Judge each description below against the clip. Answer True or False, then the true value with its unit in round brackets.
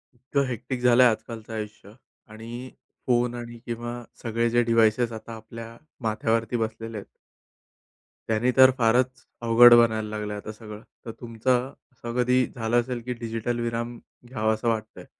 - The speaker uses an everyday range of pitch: False (1.4 semitones)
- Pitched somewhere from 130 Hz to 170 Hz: False (115 Hz)